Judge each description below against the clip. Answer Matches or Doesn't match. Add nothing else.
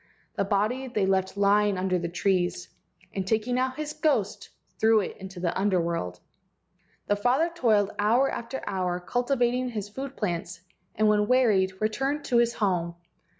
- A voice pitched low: Doesn't match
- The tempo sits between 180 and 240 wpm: Doesn't match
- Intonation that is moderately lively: Matches